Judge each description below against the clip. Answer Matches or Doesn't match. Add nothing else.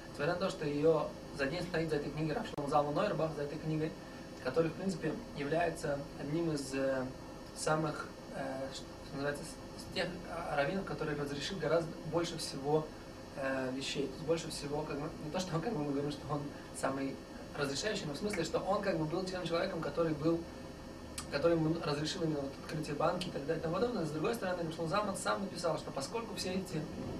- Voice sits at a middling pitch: Matches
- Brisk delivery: Matches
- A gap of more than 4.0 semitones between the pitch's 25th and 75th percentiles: Doesn't match